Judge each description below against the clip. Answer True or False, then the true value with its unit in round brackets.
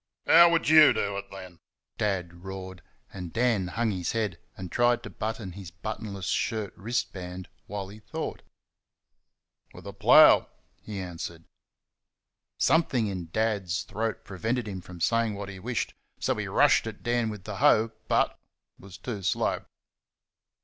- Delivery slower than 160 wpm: True (150 wpm)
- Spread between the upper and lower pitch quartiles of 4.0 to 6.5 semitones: False (3.4 semitones)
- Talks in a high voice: False (100 Hz)